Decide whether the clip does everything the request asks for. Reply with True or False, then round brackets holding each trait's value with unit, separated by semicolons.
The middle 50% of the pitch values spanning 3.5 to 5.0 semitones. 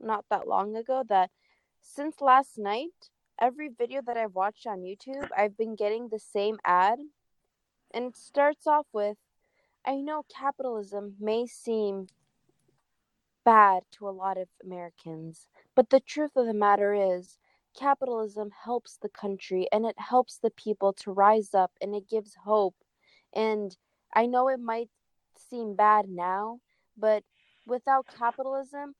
True (4.1 semitones)